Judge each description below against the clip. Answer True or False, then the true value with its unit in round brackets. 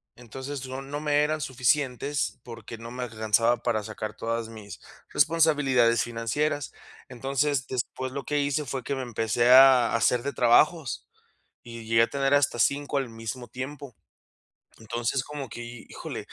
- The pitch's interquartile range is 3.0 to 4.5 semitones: True (3.4 semitones)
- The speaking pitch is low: True (125 Hz)